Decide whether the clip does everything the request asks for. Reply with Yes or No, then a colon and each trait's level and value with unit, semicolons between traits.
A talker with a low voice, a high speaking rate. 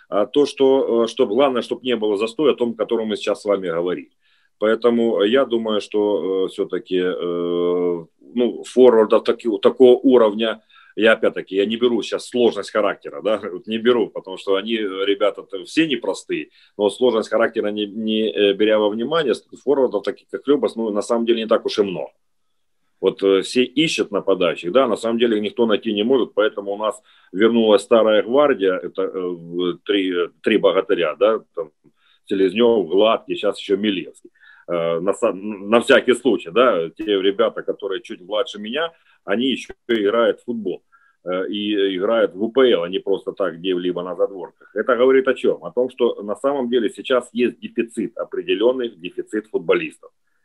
Yes: low, 120 Hz; fast, 165 wpm